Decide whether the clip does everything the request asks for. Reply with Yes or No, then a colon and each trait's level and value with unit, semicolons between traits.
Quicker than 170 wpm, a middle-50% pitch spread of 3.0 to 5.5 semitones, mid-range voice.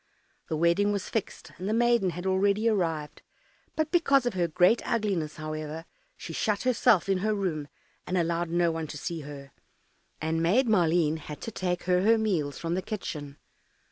Yes: average, 180 wpm; average, 4.6 semitones; medium, 180 Hz